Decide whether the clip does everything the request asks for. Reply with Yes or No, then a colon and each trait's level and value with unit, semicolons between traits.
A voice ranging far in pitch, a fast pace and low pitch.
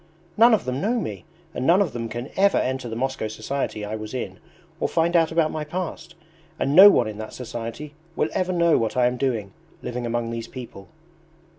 Yes: wide, 6.3 semitones; fast, 210 wpm; low, 130 Hz